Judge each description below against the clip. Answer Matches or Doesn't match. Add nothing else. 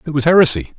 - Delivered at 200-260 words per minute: Matches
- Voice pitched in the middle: Matches